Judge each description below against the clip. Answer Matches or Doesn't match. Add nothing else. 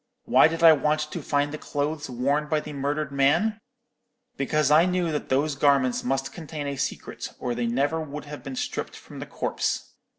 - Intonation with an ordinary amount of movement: Doesn't match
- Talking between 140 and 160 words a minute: Doesn't match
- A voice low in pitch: Doesn't match